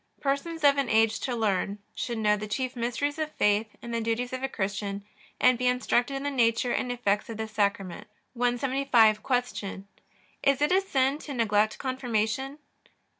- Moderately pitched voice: No, high, 240 Hz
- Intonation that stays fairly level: No, average, 3.8 semitones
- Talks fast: No, average, 175 wpm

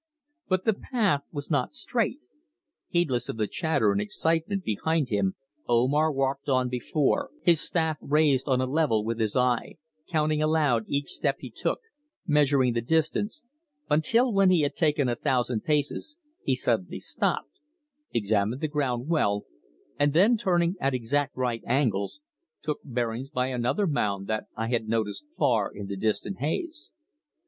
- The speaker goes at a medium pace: Yes, average, 155 wpm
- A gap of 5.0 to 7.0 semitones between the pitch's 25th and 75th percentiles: Yes, average, 5.3 semitones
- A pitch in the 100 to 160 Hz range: Yes, medium, 140 Hz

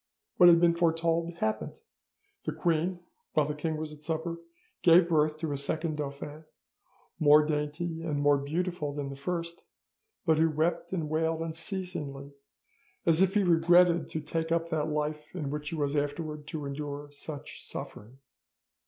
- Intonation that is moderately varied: No, narrow, 2.2 semitones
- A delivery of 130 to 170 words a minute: Yes, average, 160 wpm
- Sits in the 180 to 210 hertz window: No, medium, 155 Hz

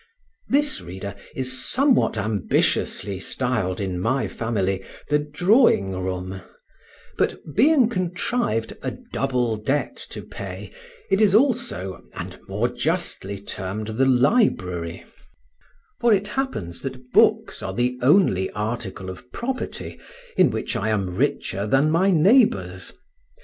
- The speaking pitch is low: Yes, low, 125 Hz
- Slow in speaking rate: Yes, slow, 125 wpm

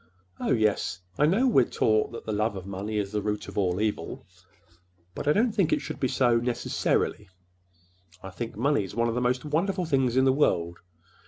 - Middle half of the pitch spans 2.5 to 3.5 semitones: No, average, 5.2 semitones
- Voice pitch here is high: No, low, 115 Hz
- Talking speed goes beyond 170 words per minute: Yes, average, 190 wpm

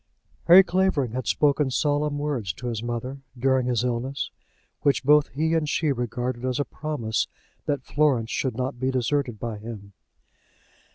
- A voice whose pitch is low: Yes, low, 130 Hz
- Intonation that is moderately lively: Yes, average, 3.5 semitones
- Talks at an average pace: Yes, average, 160 wpm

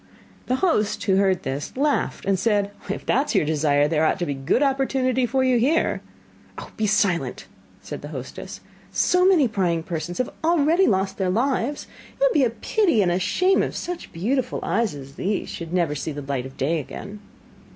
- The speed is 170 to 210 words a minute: Yes, average, 195 wpm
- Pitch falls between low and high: No, high, 205 Hz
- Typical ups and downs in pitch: No, wide, 8.1 semitones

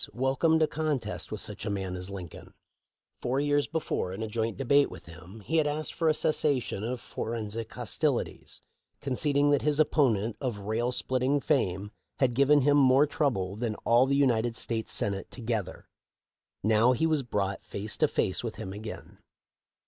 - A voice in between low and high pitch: No, low, 120 Hz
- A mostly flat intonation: No, wide, 5.5 semitones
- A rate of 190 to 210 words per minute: No, average, 175 wpm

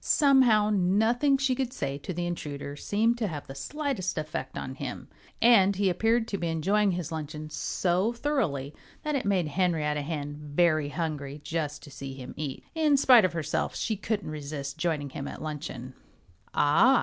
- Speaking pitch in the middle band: Yes, medium, 170 Hz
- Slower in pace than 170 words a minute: No, average, 175 wpm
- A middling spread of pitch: No, wide, 7.0 semitones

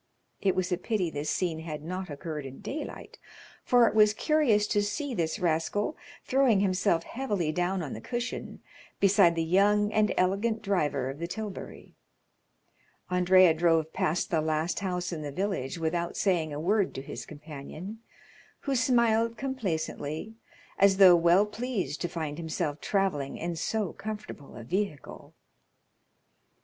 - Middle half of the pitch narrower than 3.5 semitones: No, average, 4.7 semitones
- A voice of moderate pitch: Yes, medium, 180 Hz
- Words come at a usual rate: Yes, average, 150 wpm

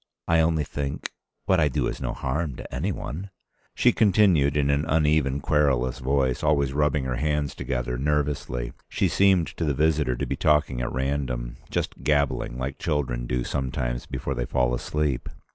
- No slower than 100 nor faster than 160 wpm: No, average, 175 wpm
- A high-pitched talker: No, very low, 70 Hz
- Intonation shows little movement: No, average, 3.1 semitones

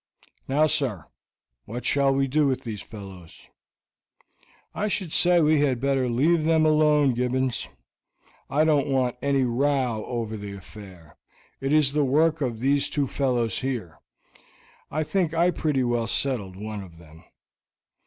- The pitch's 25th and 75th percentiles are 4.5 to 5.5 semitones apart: Yes, average, 4.8 semitones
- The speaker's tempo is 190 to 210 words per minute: No, average, 150 wpm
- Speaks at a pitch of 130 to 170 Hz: Yes, low, 135 Hz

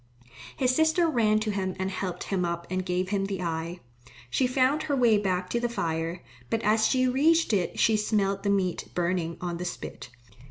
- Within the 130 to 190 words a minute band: No, average, 200 wpm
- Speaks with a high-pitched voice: Yes, high, 200 Hz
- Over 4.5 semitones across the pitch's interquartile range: Yes, average, 5.0 semitones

